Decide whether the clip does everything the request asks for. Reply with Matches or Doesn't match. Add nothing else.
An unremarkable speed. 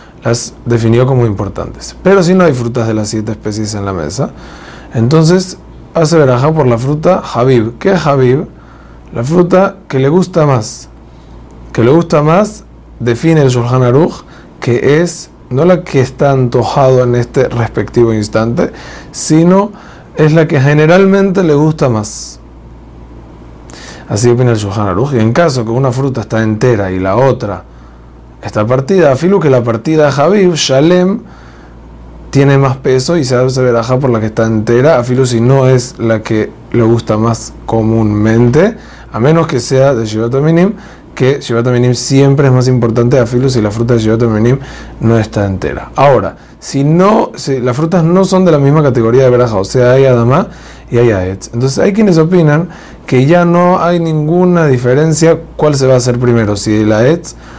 Matches